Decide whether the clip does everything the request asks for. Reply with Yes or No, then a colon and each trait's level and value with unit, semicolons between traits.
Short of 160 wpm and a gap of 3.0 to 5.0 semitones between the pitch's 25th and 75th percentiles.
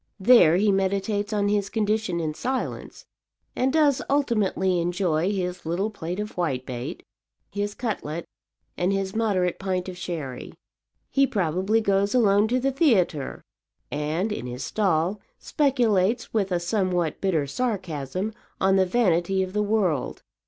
Yes: average, 140 wpm; average, 3.8 semitones